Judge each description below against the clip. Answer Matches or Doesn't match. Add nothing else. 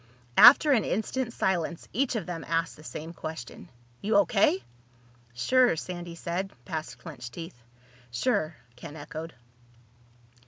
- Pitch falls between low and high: Matches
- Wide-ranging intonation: Doesn't match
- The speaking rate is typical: Doesn't match